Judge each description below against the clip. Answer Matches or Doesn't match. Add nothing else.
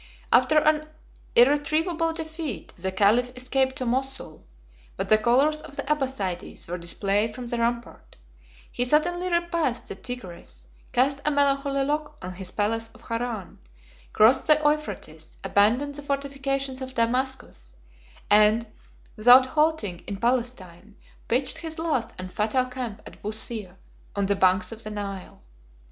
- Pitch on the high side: Matches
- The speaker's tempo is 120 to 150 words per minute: Matches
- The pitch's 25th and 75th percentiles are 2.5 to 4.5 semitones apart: Doesn't match